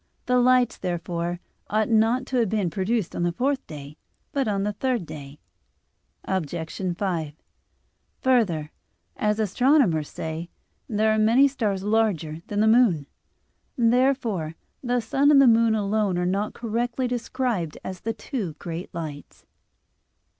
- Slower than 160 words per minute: Yes, average, 140 wpm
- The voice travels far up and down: Yes, wide, 5.9 semitones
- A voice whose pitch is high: Yes, high, 210 Hz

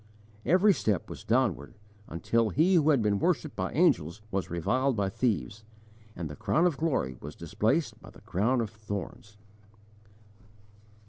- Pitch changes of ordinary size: No, wide, 6.3 semitones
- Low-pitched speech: Yes, low, 110 Hz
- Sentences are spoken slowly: No, average, 150 wpm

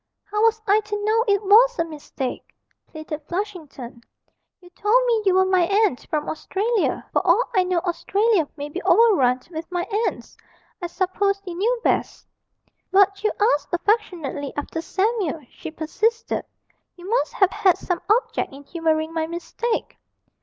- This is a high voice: Yes, very high, 375 Hz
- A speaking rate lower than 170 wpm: Yes, average, 160 wpm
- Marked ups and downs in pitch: No, average, 4.7 semitones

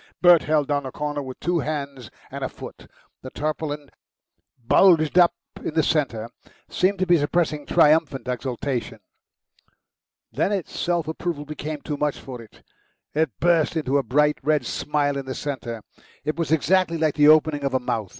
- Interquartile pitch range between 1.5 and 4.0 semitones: Yes, average, 2.7 semitones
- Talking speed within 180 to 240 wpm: No, average, 170 wpm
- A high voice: No, medium, 150 Hz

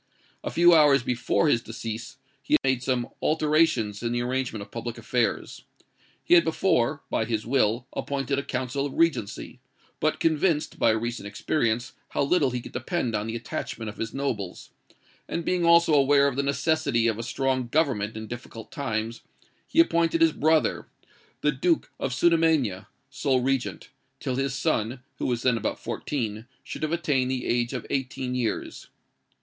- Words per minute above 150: Yes, average, 170 wpm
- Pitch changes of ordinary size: Yes, average, 4.2 semitones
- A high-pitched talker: No, low, 130 Hz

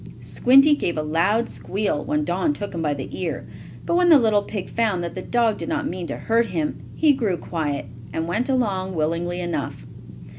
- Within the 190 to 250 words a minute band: Yes, average, 200 wpm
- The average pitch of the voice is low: No, medium, 185 Hz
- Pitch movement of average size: No, wide, 5.7 semitones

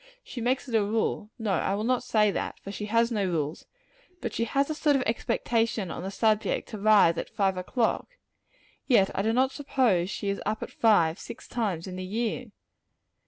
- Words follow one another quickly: Yes, fast, 210 wpm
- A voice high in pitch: Yes, high, 215 Hz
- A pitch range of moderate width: Yes, average, 3.5 semitones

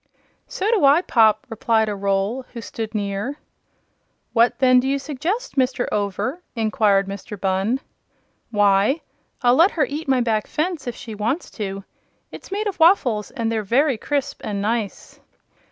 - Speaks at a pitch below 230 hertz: No, high, 235 Hz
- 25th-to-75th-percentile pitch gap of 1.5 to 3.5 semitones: No, average, 5.0 semitones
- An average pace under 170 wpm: Yes, average, 160 wpm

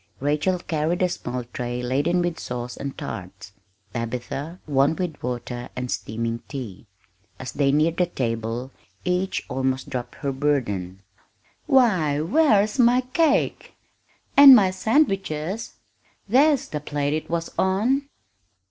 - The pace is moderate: No, slow, 130 wpm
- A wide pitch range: Yes, wide, 7.2 semitones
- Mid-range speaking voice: Yes, medium, 150 Hz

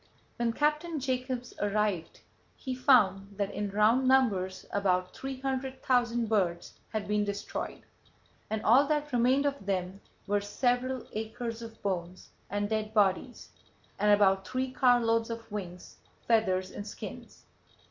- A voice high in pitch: Yes, high, 220 Hz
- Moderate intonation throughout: Yes, average, 4.2 semitones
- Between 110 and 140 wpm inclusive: Yes, slow, 135 wpm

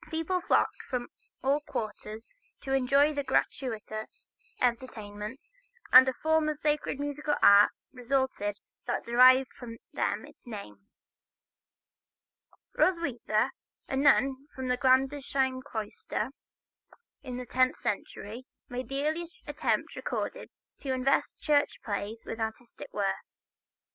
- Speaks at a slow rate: Yes, slow, 120 wpm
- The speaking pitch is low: No, very high, 260 Hz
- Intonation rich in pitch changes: No, average, 3.7 semitones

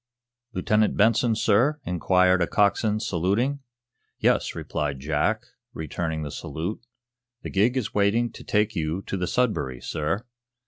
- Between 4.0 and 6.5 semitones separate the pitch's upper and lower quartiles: Yes, average, 5.2 semitones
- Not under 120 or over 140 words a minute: Yes, slow, 135 wpm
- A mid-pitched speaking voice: No, low, 100 Hz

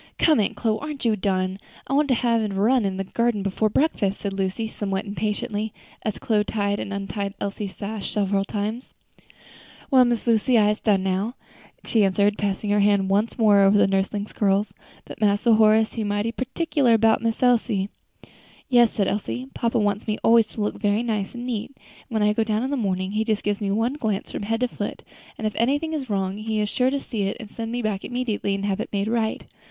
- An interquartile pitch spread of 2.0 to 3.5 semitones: Yes, narrow, 2.5 semitones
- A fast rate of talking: Yes, fast, 220 wpm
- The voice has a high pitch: Yes, high, 215 Hz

